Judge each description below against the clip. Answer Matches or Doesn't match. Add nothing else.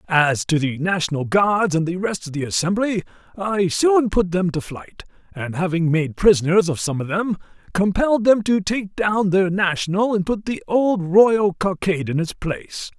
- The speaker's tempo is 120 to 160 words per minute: Doesn't match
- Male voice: Matches